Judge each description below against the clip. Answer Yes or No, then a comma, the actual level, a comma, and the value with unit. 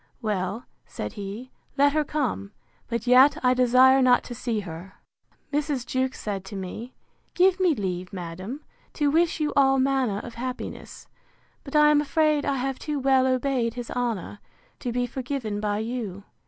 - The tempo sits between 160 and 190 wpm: Yes, average, 170 wpm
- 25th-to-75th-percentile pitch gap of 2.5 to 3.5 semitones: No, average, 4.6 semitones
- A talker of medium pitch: No, very high, 250 Hz